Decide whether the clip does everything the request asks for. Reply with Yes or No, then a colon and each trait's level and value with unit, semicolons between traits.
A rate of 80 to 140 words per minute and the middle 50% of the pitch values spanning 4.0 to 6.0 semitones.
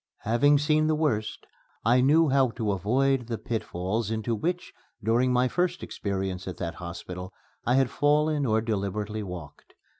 No: average, 155 wpm; wide, 5.5 semitones